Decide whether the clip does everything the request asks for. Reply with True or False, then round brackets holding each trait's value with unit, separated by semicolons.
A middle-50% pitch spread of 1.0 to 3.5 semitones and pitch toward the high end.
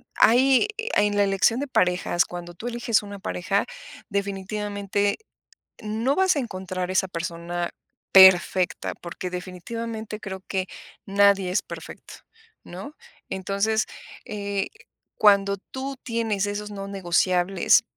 True (2.7 semitones; 200 Hz)